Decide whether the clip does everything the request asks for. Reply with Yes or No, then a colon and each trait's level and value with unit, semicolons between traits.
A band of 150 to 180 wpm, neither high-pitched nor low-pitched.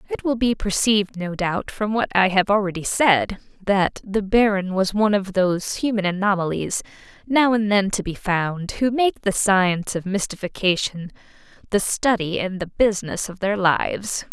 No: average, 170 wpm; high, 195 Hz